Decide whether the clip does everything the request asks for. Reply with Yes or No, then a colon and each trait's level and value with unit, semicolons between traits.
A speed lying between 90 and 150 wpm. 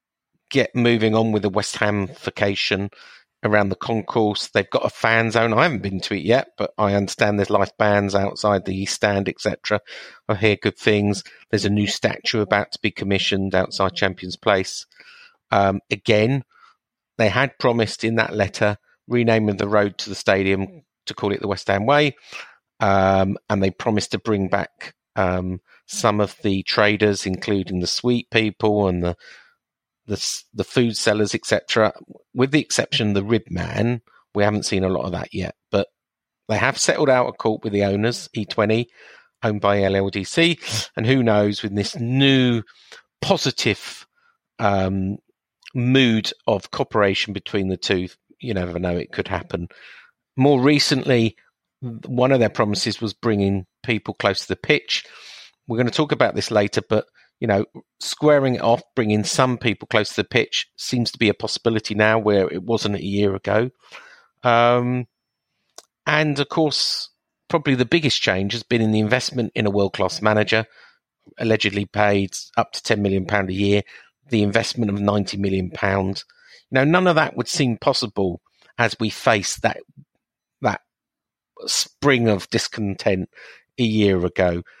No: average, 165 wpm